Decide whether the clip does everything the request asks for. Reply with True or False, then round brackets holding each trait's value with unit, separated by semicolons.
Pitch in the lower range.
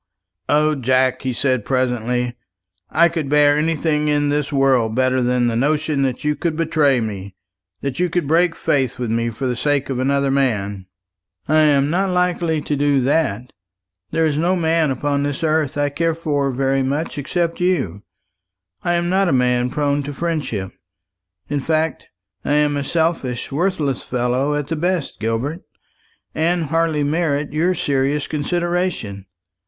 False (145 Hz)